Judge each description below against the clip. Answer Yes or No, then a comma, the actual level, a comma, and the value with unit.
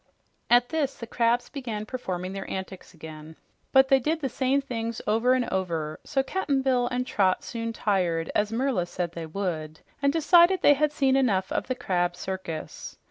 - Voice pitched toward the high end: Yes, high, 230 Hz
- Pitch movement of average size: No, wide, 6.4 semitones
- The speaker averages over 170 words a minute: Yes, average, 185 wpm